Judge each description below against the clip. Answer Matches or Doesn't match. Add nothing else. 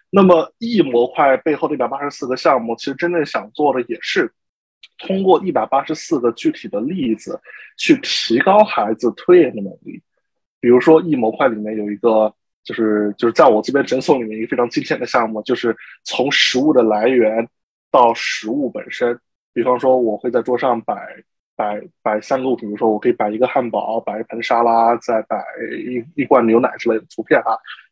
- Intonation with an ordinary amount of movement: Doesn't match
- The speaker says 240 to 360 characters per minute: Matches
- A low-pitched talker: Matches